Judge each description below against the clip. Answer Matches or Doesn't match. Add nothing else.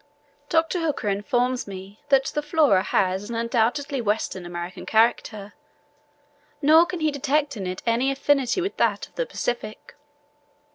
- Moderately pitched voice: Doesn't match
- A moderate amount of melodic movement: Doesn't match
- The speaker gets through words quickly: Doesn't match